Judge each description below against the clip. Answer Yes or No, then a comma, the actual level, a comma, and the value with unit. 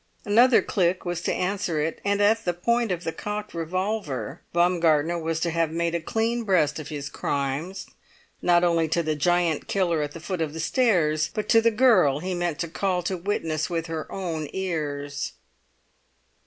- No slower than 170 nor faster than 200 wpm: Yes, average, 185 wpm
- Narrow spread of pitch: No, average, 3.5 semitones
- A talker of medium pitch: Yes, medium, 170 Hz